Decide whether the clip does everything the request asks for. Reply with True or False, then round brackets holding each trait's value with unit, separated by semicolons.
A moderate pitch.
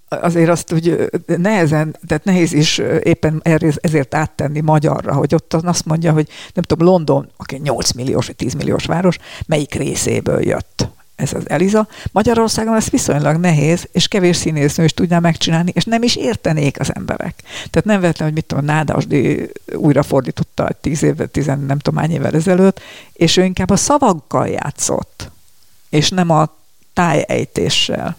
True (160 Hz)